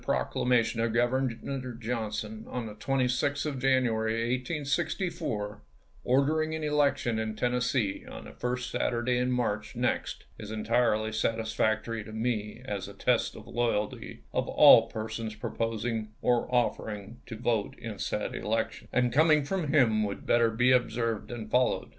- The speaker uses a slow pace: No, average, 150 wpm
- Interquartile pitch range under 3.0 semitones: Yes, narrow, 2.5 semitones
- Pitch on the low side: Yes, low, 120 Hz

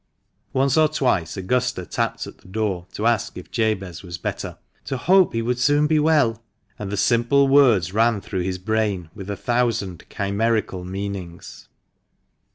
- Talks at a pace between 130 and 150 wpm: No, average, 165 wpm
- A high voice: No, low, 110 Hz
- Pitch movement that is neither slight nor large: Yes, average, 4.8 semitones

